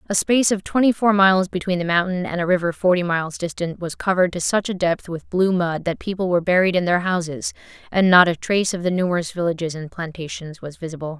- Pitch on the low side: No, medium, 175 Hz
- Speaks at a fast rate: Yes, fast, 230 wpm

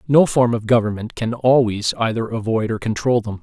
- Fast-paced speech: No, average, 195 wpm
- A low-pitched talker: Yes, low, 115 Hz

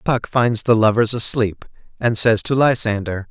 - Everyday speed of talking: Yes, average, 165 wpm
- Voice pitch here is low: Yes, low, 115 Hz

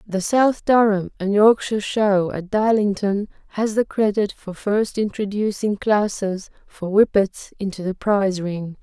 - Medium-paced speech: Yes, average, 145 wpm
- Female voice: Yes, female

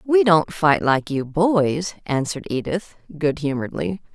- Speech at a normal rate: Yes, average, 145 wpm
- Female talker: Yes, female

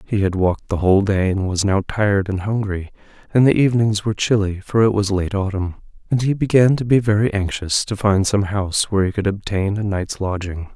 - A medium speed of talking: No, fast, 225 wpm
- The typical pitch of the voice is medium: No, low, 100 Hz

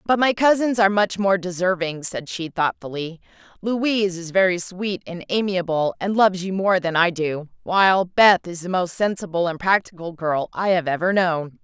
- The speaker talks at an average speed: Yes, average, 185 wpm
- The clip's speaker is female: Yes, female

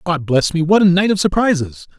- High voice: No, medium, 170 Hz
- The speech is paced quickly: Yes, fast, 240 wpm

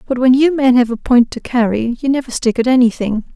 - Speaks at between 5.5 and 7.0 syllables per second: Yes, 5.8 syllables/s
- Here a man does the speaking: No, female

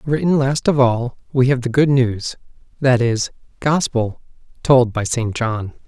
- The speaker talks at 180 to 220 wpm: No, average, 155 wpm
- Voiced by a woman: No, male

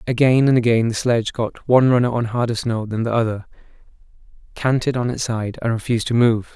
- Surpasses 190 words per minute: Yes, average, 200 wpm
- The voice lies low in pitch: Yes, low, 120 Hz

